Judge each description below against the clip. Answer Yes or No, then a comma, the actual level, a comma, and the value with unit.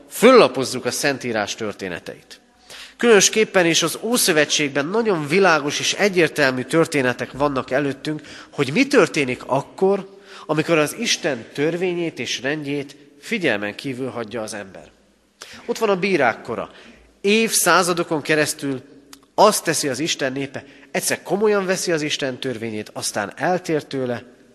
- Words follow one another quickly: No, average, 125 wpm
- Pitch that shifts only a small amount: No, wide, 5.5 semitones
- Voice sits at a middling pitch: Yes, medium, 150 Hz